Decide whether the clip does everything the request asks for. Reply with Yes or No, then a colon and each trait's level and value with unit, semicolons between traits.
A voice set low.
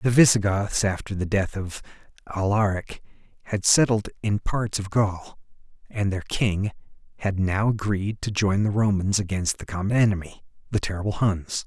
Yes: low, 100 Hz